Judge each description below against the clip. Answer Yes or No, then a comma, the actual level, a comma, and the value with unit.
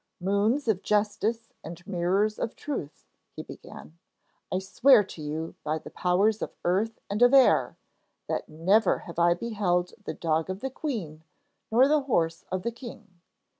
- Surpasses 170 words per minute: No, average, 165 wpm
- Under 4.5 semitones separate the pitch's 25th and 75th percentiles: No, average, 4.8 semitones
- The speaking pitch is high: Yes, high, 195 Hz